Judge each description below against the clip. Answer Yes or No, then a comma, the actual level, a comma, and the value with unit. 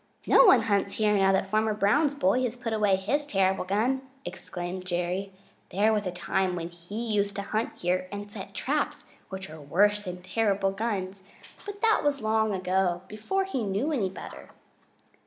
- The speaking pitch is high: Yes, high, 200 Hz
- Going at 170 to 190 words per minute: Yes, average, 180 wpm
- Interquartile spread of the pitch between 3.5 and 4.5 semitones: No, average, 2.9 semitones